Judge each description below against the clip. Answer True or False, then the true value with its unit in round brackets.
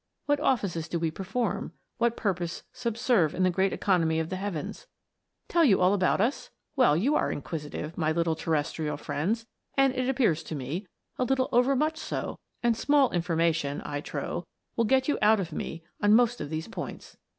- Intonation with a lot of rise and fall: True (7.1 semitones)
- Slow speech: False (195 wpm)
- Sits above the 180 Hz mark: True (190 Hz)